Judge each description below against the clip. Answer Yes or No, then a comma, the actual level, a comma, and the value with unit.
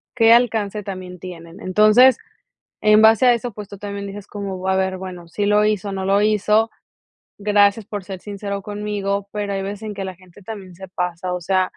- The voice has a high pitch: Yes, high, 200 Hz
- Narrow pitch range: Yes, narrow, 1.9 semitones